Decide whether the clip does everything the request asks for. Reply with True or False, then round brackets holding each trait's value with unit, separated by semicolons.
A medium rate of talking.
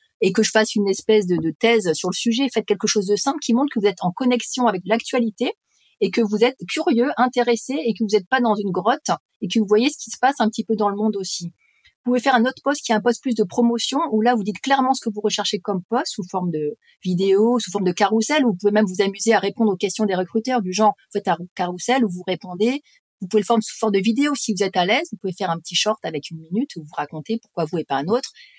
False (290 wpm)